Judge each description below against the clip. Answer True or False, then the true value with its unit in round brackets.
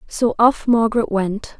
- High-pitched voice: True (220 Hz)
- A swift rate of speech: False (150 wpm)